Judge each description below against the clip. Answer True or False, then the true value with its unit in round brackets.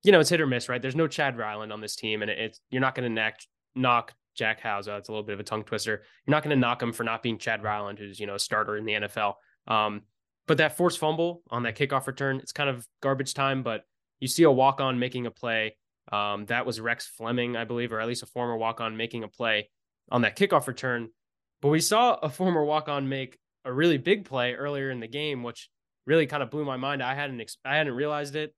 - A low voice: True (125 Hz)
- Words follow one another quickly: True (255 wpm)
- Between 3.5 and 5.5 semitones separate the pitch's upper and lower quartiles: True (4.4 semitones)